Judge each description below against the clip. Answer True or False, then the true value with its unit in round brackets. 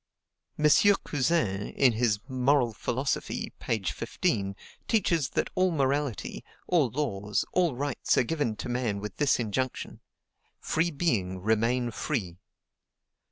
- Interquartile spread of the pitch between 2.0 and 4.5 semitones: False (5.5 semitones)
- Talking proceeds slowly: True (120 wpm)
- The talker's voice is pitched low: True (125 Hz)